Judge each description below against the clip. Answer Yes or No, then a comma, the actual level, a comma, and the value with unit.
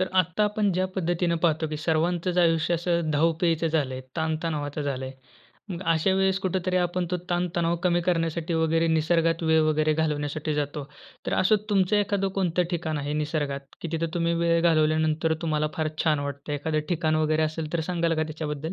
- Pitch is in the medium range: Yes, medium, 165 Hz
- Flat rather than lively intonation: Yes, narrow, 2.0 semitones